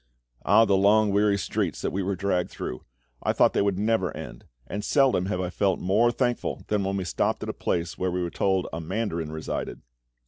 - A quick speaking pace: Yes, fast, 215 wpm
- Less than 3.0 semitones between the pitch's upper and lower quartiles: Yes, narrow, 2.6 semitones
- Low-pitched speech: Yes, very low, 95 Hz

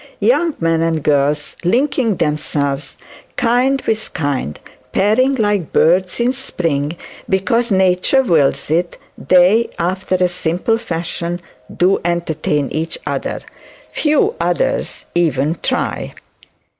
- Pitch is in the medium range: Yes, medium, 180 Hz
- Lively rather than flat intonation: Yes, wide, 6.4 semitones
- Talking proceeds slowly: Yes, slow, 110 wpm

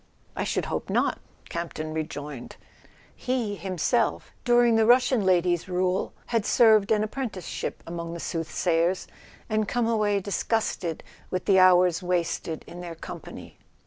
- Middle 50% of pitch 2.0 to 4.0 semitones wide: No, average, 4.5 semitones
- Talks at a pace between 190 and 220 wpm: No, average, 145 wpm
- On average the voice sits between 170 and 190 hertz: Yes, medium, 185 Hz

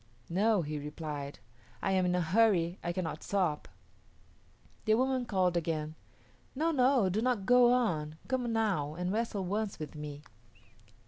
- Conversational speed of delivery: Yes, average, 150 wpm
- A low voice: No, medium, 185 Hz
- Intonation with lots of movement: Yes, wide, 6.2 semitones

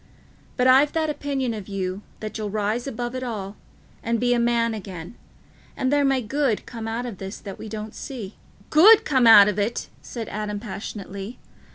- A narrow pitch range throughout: No, average, 3.7 semitones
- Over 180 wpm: Yes, average, 190 wpm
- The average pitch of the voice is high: Yes, high, 225 Hz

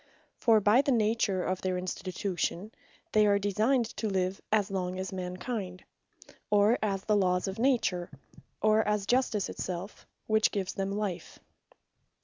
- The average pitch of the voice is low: No, high, 200 Hz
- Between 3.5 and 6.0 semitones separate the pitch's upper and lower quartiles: No, average, 2.7 semitones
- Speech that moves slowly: No, average, 155 wpm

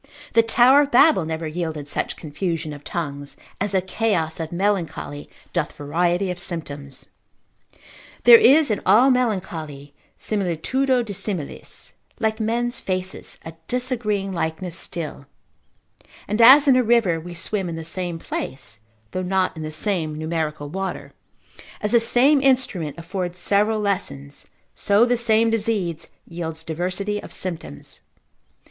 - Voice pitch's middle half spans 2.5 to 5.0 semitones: No, wide, 5.6 semitones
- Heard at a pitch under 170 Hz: No, medium, 185 Hz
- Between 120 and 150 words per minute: Yes, average, 140 wpm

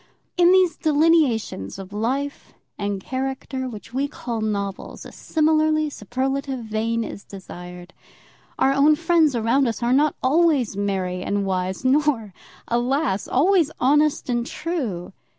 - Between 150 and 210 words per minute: No, slow, 135 wpm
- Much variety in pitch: Yes, wide, 6.5 semitones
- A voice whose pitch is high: Yes, very high, 255 Hz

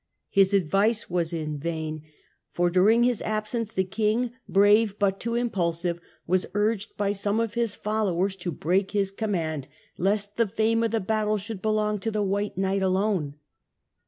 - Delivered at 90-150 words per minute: No, average, 175 wpm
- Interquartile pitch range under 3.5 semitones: Yes, average, 2.8 semitones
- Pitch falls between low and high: No, high, 200 Hz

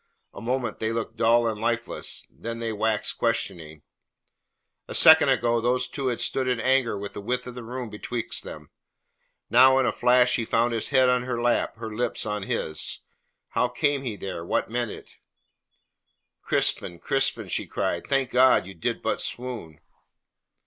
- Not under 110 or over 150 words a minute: No, average, 175 wpm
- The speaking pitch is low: Yes, low, 120 Hz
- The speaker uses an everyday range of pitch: No, narrow, 2.3 semitones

